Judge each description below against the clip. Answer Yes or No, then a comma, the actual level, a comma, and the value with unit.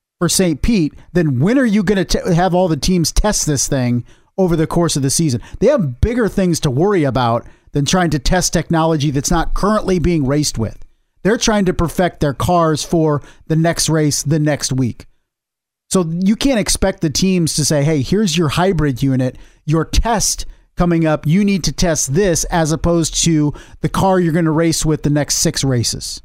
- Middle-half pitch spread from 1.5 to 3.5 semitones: No, average, 3.9 semitones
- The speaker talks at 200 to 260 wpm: Yes, fast, 205 wpm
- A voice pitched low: No, medium, 160 Hz